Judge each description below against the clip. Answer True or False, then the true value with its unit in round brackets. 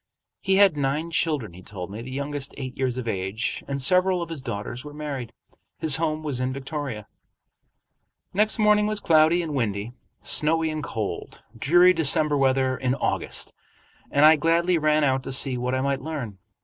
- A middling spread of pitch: True (4.1 semitones)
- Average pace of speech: True (180 wpm)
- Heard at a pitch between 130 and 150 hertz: True (140 Hz)